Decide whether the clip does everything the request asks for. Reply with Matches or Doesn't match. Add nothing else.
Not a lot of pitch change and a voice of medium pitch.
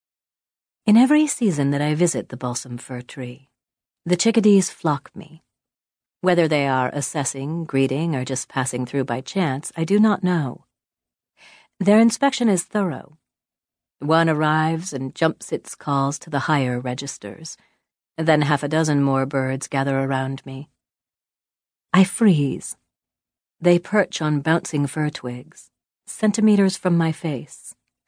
Doesn't match